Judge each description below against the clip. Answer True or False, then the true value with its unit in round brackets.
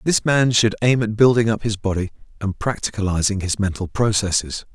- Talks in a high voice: False (105 Hz)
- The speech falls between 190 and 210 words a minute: False (175 wpm)